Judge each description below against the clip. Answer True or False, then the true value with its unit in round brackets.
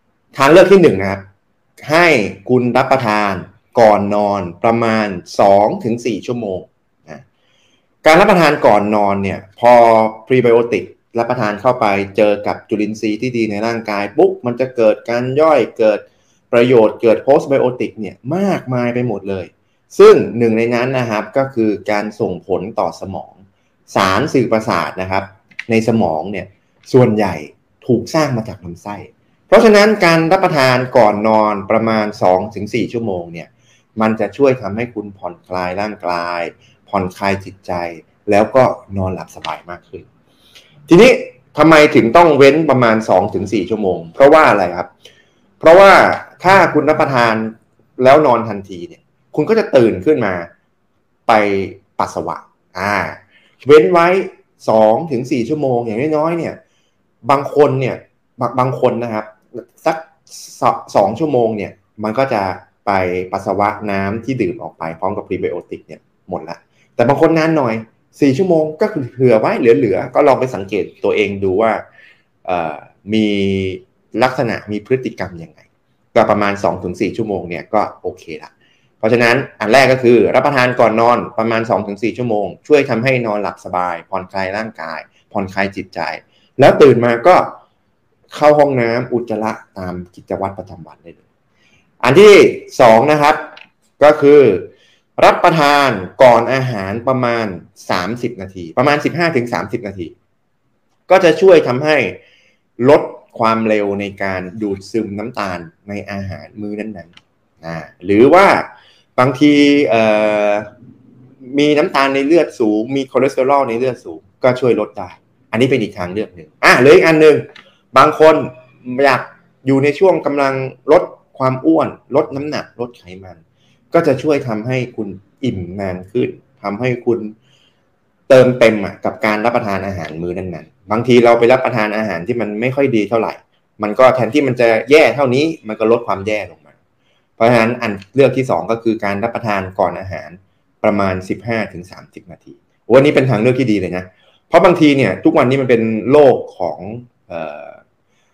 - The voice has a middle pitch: False (115 Hz)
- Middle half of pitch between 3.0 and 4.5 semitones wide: False (5.0 semitones)